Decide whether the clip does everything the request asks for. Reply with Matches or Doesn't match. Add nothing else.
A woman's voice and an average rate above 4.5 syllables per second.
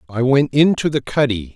Doesn't match